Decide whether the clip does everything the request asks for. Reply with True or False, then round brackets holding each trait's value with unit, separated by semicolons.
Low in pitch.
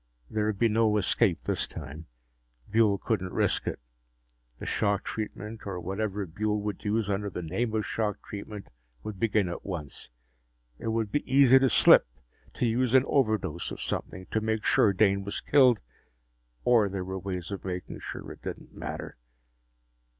True (105 Hz)